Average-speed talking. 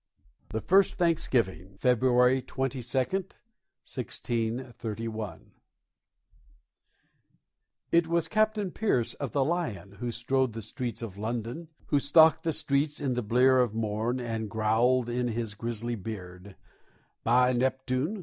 No: slow, 120 wpm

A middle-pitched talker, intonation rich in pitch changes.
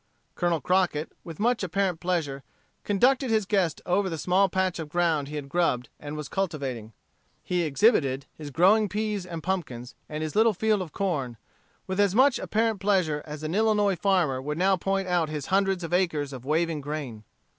No: medium, 175 Hz; average, 4.7 semitones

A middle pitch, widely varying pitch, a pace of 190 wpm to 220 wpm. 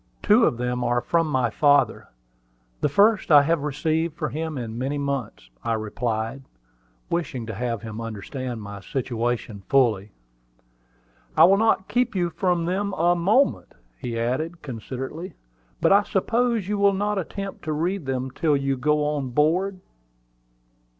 No: medium, 145 Hz; wide, 6.6 semitones; average, 155 wpm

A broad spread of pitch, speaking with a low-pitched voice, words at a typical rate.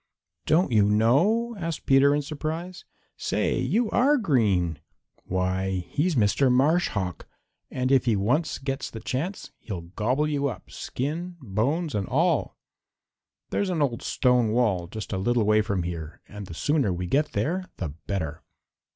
Yes: wide, 7.6 semitones; low, 125 Hz; average, 160 wpm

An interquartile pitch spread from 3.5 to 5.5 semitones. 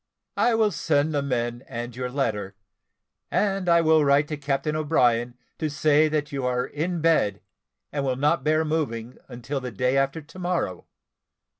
Yes: average, 4.0 semitones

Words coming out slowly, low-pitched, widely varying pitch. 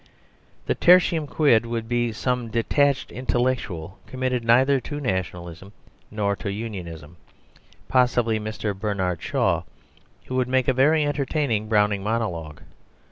No: slow, 125 wpm; low, 115 Hz; average, 4.3 semitones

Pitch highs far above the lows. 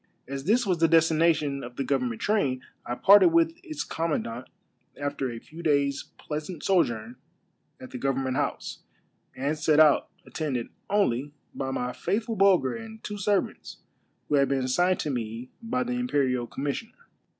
Yes: wide, 7.0 semitones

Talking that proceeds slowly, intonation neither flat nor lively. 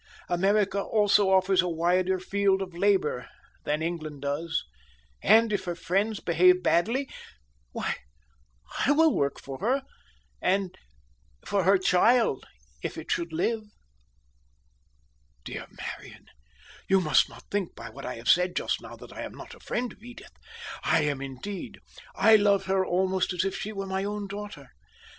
No: average, 155 wpm; average, 3.2 semitones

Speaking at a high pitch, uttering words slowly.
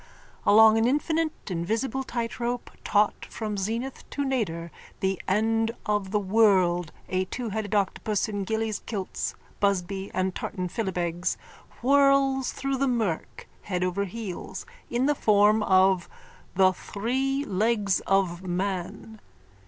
Yes: high, 210 Hz; slow, 125 wpm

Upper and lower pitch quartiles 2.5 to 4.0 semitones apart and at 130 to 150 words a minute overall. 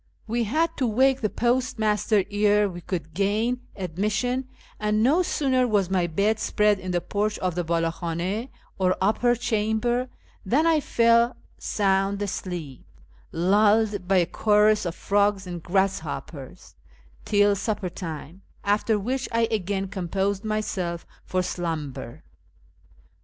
Yes: average, 3.4 semitones; slow, 135 wpm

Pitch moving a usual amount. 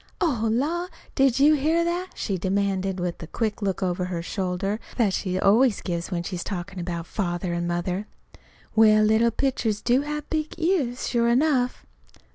No: wide, 6.5 semitones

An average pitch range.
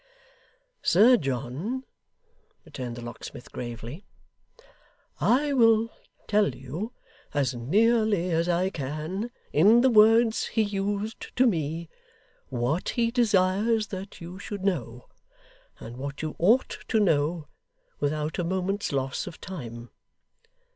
No: wide, 7.4 semitones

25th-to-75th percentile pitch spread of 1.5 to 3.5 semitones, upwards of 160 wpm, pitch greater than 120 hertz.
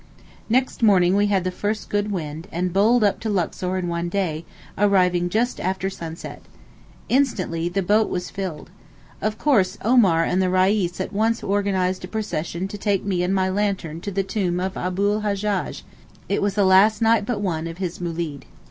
Yes: narrow, 2.6 semitones; average, 185 wpm; high, 190 Hz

